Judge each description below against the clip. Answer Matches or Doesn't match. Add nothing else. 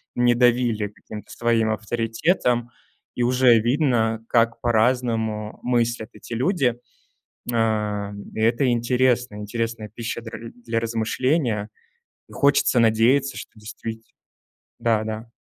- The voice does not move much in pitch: Matches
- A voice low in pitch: Matches